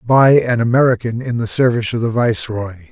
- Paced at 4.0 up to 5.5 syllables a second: No, 5.9 syllables/s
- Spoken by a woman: No, male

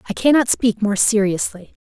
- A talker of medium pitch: No, high, 220 Hz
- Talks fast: No, average, 165 wpm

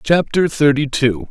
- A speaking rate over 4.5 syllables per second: No, 4.1 syllables/s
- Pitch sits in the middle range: Yes, medium, 145 Hz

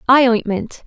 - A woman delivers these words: Yes, female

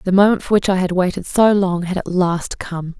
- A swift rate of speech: Yes, fast, 260 wpm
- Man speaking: No, female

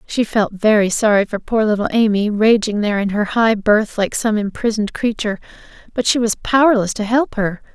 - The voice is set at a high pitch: Yes, high, 215 Hz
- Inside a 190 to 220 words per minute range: Yes, average, 195 wpm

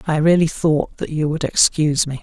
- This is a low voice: No, medium, 155 Hz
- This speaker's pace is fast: Yes, fast, 215 wpm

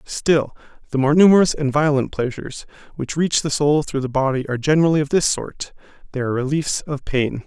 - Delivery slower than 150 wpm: No, average, 185 wpm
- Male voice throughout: Yes, male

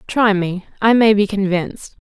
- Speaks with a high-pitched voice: Yes, high, 205 Hz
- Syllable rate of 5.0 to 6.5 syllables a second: No, 4.7 syllables/s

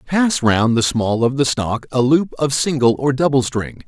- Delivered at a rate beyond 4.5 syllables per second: No, 4.4 syllables/s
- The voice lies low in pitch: Yes, low, 130 Hz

